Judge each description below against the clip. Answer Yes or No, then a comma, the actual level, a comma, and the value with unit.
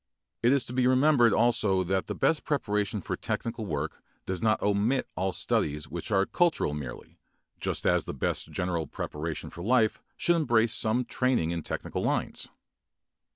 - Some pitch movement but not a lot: No, wide, 6.1 semitones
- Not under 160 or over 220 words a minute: Yes, average, 165 wpm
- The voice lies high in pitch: No, low, 105 Hz